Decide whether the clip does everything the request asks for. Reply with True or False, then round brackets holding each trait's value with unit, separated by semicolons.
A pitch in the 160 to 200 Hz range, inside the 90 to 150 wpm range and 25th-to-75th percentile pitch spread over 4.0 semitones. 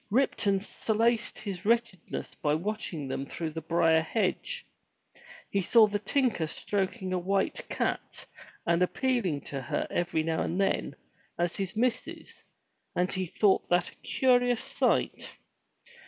True (190 Hz; 140 wpm; 5.0 semitones)